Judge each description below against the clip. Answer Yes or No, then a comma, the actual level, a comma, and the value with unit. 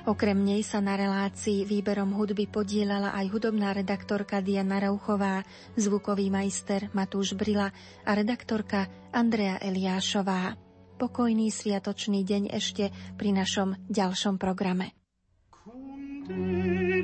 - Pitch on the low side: No, high, 200 Hz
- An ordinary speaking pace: No, slow, 100 wpm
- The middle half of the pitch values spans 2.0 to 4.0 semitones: No, narrow, 1.4 semitones